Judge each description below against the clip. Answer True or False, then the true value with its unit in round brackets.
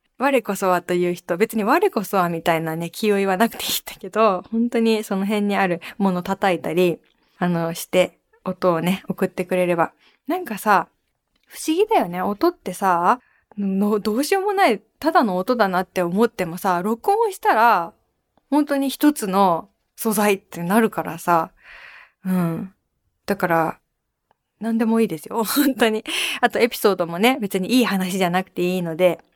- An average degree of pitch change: True (4.5 semitones)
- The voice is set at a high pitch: True (200 Hz)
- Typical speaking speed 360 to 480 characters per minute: False (325 characters per minute)